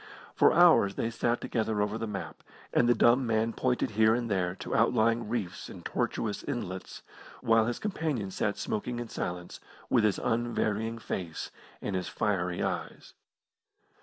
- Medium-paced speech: Yes, average, 160 wpm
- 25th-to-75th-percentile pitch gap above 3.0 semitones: No, average, 2.7 semitones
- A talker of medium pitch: No, low, 110 Hz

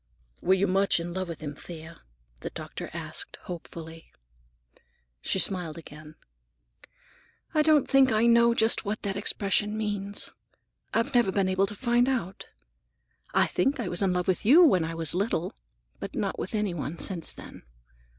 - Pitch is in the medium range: No, high, 195 Hz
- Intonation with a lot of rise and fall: No, average, 4.9 semitones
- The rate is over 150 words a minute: Yes, average, 170 wpm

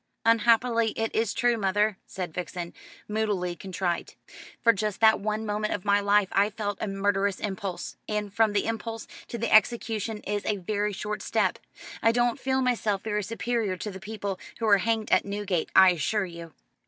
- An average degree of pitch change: No, narrow, 2.3 semitones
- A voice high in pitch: Yes, high, 210 Hz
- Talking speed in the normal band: Yes, average, 180 wpm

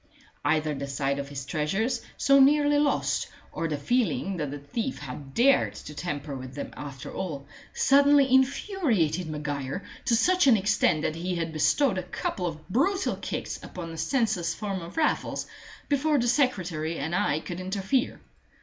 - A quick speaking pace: No, average, 170 wpm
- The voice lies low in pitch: No, medium, 180 Hz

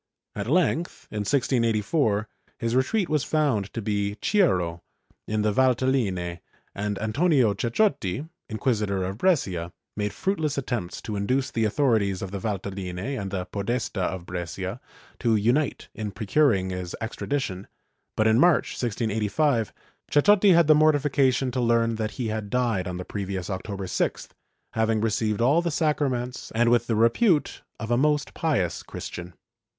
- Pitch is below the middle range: Yes, low, 115 Hz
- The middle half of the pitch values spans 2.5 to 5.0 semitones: No, wide, 5.5 semitones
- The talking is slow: No, average, 155 wpm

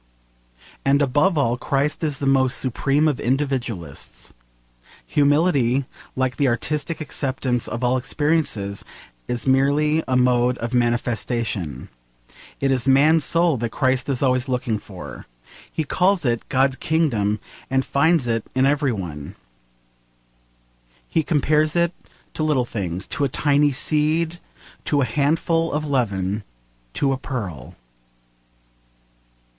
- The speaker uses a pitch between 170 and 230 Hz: No, low, 135 Hz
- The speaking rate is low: Yes, slow, 130 wpm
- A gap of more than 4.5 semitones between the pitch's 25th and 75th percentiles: No, average, 3.8 semitones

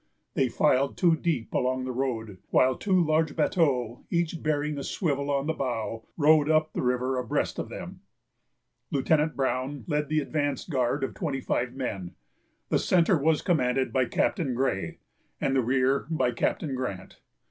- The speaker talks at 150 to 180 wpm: Yes, average, 165 wpm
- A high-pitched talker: No, low, 135 Hz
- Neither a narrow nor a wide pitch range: Yes, average, 3.4 semitones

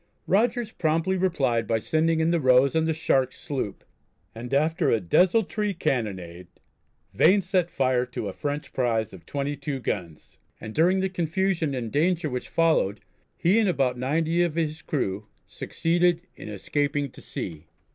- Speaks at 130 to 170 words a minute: Yes, average, 155 wpm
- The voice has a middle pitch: Yes, medium, 150 Hz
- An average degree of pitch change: No, wide, 5.8 semitones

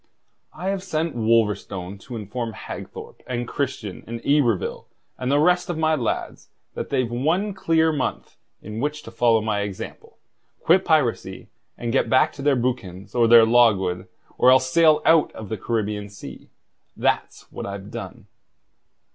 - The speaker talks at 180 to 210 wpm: No, average, 160 wpm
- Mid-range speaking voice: No, low, 120 Hz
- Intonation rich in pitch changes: Yes, wide, 5.9 semitones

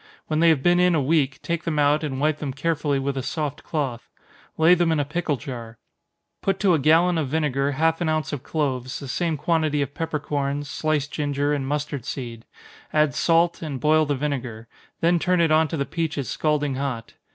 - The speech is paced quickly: Yes, fast, 210 wpm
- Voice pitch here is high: No, medium, 150 Hz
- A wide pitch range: No, average, 2.7 semitones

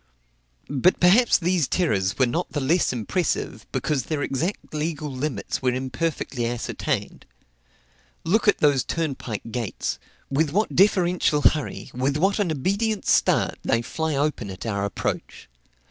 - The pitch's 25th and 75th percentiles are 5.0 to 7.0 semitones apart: Yes, wide, 5.5 semitones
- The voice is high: No, medium, 150 Hz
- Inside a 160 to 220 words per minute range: No, average, 140 wpm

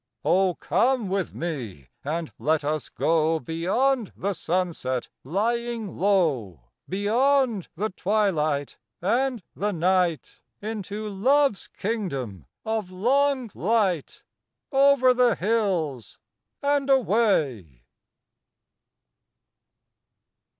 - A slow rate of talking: Yes, slow, 85 wpm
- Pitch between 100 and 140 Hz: No, high, 195 Hz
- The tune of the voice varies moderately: No, wide, 6.5 semitones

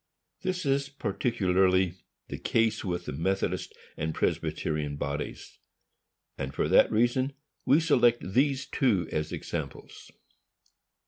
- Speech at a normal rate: No, slow, 115 wpm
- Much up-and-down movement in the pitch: Yes, wide, 7.3 semitones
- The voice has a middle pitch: No, low, 100 Hz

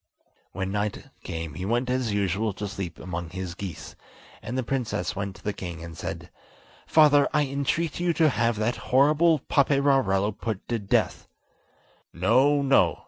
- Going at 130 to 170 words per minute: Yes, average, 160 wpm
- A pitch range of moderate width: No, wide, 6.4 semitones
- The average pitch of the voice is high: No, low, 110 Hz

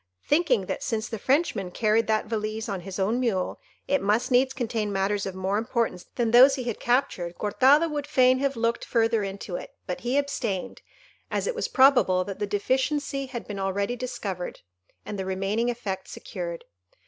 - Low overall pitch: No, high, 225 Hz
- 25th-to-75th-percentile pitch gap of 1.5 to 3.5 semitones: No, average, 4.6 semitones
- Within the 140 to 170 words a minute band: No, average, 185 wpm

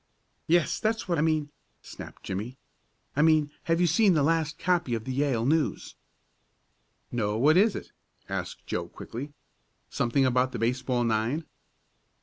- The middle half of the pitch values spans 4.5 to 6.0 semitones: Yes, average, 5.0 semitones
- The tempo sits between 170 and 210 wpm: No, average, 150 wpm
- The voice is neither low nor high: Yes, medium, 145 Hz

